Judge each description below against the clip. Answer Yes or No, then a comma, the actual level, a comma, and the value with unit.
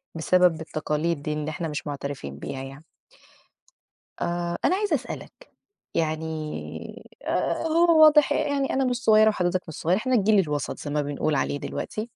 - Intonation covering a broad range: Yes, wide, 8.2 semitones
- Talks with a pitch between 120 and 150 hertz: No, medium, 170 Hz